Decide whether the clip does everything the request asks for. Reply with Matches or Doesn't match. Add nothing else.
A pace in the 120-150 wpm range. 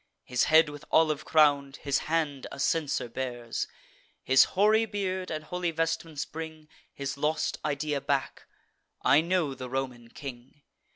Matches